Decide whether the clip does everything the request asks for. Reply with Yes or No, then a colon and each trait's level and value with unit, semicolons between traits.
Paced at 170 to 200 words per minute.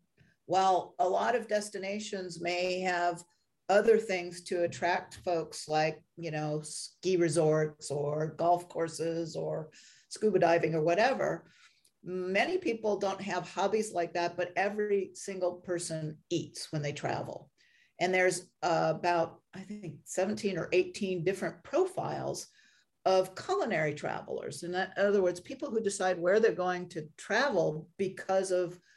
No: average, 145 wpm